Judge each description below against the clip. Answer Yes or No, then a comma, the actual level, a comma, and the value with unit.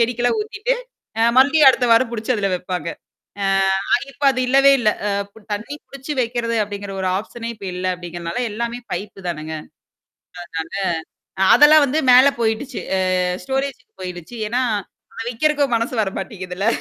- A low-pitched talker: No, high, 230 Hz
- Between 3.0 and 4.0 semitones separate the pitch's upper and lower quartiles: No, average, 5.2 semitones